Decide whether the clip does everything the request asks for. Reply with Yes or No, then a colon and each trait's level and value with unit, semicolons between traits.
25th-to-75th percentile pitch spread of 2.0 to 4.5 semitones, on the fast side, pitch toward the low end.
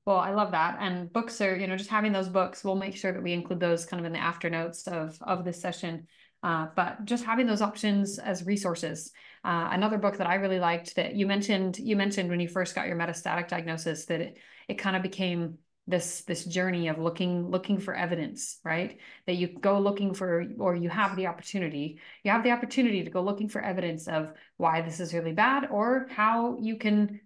No: average, 2.8 semitones; fast, 215 wpm; medium, 185 Hz